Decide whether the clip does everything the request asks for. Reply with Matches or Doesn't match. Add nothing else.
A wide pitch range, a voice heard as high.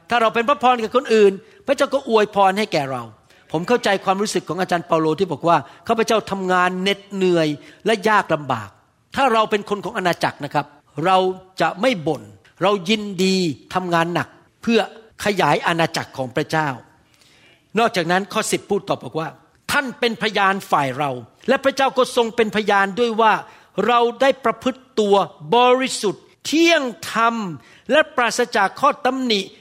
Matches